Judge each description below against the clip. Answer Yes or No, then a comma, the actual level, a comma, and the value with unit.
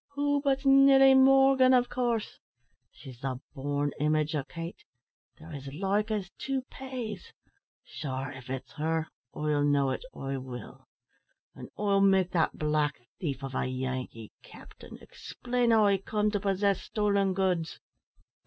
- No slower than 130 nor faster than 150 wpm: Yes, average, 145 wpm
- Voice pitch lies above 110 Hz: Yes, medium, 185 Hz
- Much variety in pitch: Yes, wide, 8.2 semitones